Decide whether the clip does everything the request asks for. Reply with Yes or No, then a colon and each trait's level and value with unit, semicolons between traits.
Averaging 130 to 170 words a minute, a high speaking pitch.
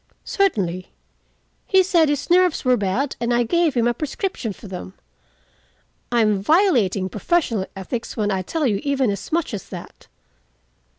Yes: average, 160 wpm; high, 240 Hz